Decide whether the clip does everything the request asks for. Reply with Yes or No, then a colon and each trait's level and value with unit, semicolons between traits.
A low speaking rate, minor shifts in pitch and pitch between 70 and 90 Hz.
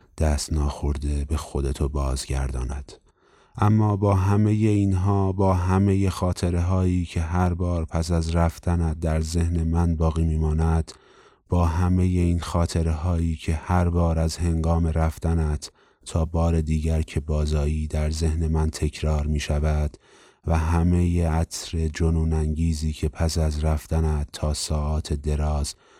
No: average, 135 wpm; narrow, 2.0 semitones; very low, 80 Hz